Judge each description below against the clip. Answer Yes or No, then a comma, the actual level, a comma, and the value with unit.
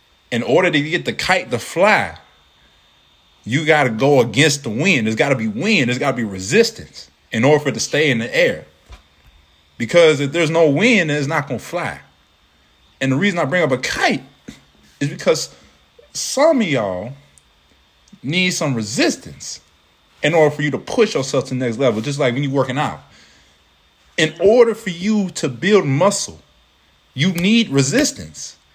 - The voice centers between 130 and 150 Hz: Yes, medium, 140 Hz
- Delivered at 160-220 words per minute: Yes, average, 185 wpm